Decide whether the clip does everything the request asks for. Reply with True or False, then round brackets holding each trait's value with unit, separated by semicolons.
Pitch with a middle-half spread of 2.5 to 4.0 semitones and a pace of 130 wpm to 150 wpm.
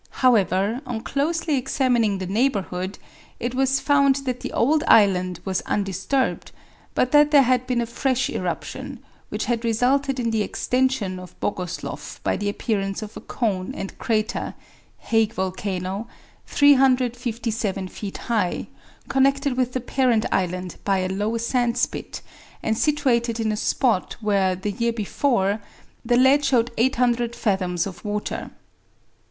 False (4.5 semitones; 145 wpm)